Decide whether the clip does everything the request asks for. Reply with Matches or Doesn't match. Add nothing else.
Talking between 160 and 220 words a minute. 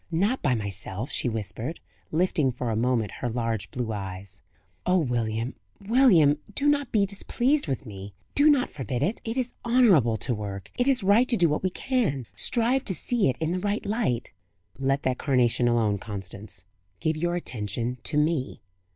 Matches